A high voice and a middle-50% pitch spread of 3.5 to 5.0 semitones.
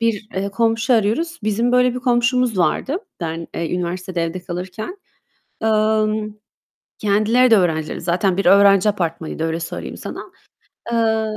Yes: high, 210 Hz; average, 4.3 semitones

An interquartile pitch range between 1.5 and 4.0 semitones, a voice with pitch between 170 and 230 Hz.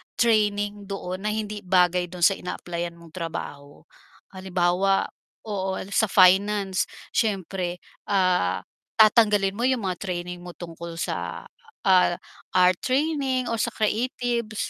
Yes: average, 3.2 semitones; high, 190 Hz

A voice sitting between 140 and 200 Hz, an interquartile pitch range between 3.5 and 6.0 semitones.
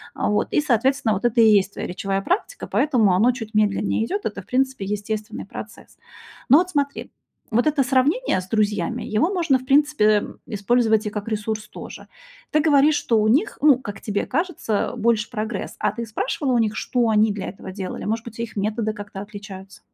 No: high, 225 Hz; average, 4.3 semitones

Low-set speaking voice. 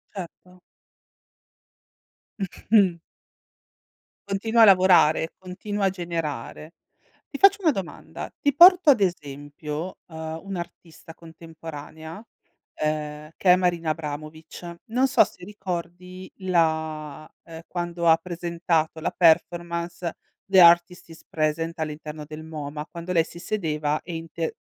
No: medium, 170 Hz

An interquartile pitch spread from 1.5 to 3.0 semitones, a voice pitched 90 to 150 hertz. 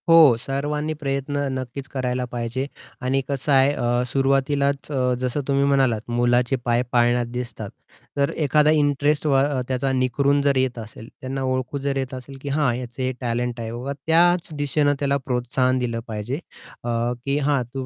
Yes: narrow, 2.4 semitones; low, 135 Hz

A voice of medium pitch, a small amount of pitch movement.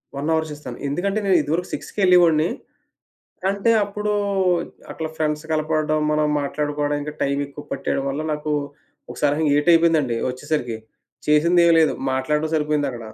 Yes: medium, 150 Hz; narrow, 2.1 semitones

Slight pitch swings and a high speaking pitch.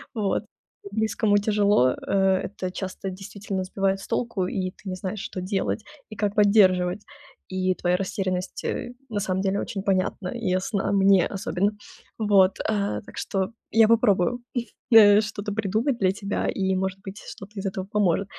Yes: narrow, 1.9 semitones; high, 195 Hz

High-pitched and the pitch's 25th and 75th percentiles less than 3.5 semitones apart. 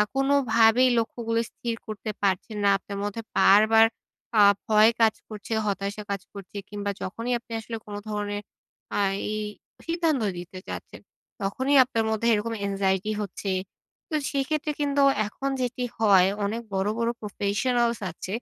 Yes: high, 220 Hz; average, 2.8 semitones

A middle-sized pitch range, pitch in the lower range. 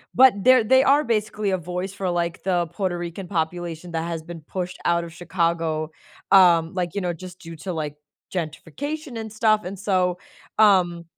No: average, 3.1 semitones; medium, 180 Hz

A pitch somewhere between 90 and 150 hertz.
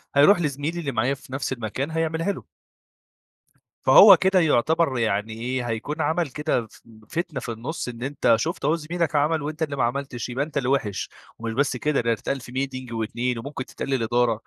Yes: low, 135 Hz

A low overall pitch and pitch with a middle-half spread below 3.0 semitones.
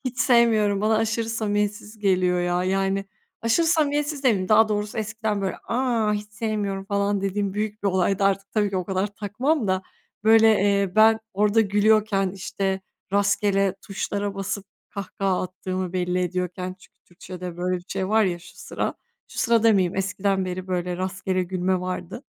No: high, 200 Hz; narrow, 2.6 semitones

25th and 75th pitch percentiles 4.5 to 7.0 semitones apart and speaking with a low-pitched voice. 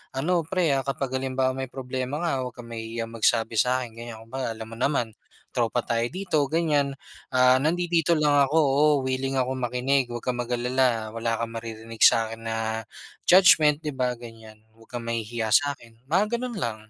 No: average, 3.7 semitones; low, 125 Hz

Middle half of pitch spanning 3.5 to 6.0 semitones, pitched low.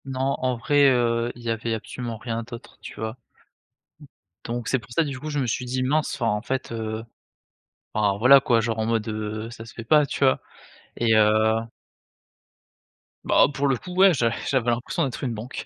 No: average, 2.9 semitones; low, 120 Hz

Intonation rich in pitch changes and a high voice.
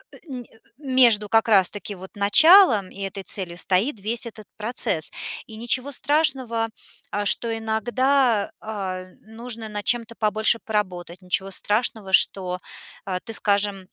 No: average, 3.4 semitones; high, 220 Hz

